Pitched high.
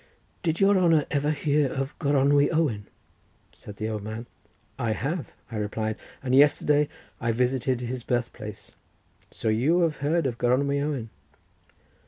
No: low, 135 Hz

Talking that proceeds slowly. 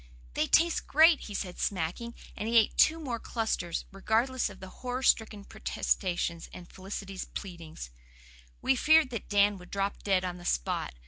No: average, 170 wpm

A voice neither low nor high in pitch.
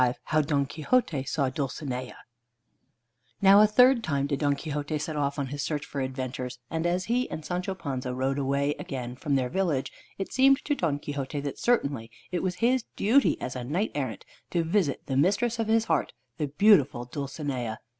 Yes: medium, 145 Hz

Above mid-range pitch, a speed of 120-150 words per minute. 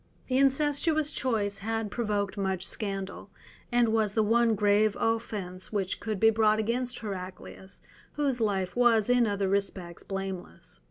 Yes: high, 215 Hz; average, 145 wpm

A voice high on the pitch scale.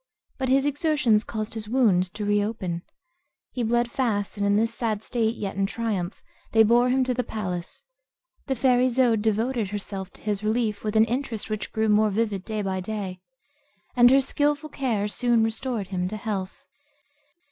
Yes: high, 220 Hz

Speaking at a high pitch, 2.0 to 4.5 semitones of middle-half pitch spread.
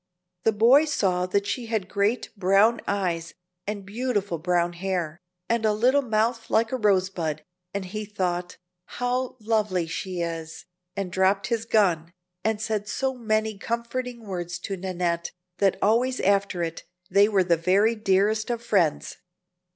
Yes: high, 200 Hz; average, 3.7 semitones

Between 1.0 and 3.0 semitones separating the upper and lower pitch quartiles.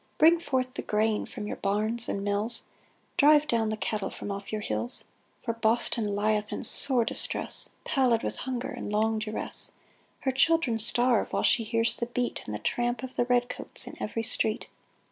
Yes: narrow, 2.6 semitones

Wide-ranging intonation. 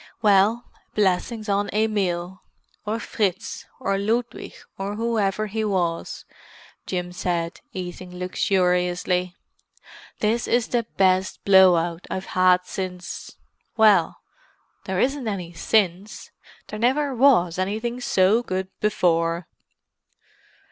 No: average, 3.4 semitones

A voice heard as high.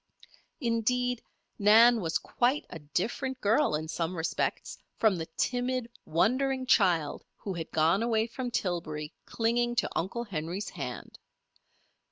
Yes: high, 220 Hz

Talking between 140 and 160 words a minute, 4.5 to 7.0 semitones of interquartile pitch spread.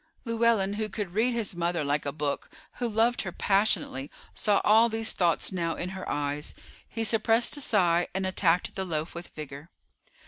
No: average, 180 wpm; average, 5.0 semitones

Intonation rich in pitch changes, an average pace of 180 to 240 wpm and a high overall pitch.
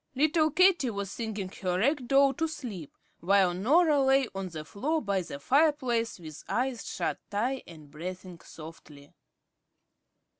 No: wide, 7.6 semitones; average, 145 wpm; high, 220 Hz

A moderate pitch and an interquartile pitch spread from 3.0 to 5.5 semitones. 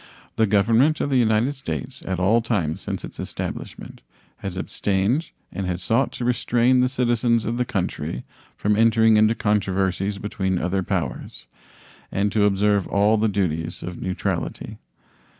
No: low, 105 Hz; average, 3.3 semitones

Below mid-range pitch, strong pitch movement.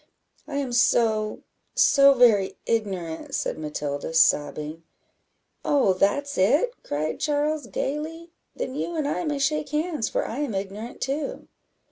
No: very high, 255 Hz; wide, 7.3 semitones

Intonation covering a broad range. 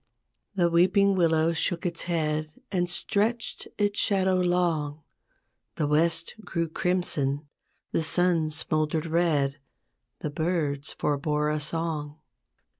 No: average, 2.8 semitones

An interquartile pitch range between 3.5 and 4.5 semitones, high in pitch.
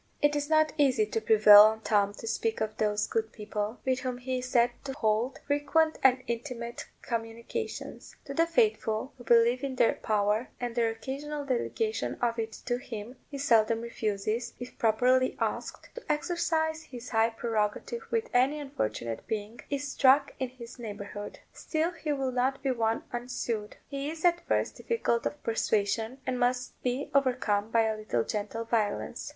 Yes: average, 3.9 semitones; high, 245 Hz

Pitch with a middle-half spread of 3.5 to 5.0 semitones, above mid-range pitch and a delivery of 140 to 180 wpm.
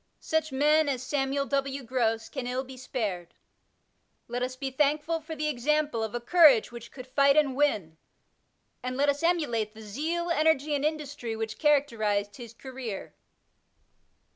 Yes: average, 4.1 semitones; very high, 270 Hz; average, 160 wpm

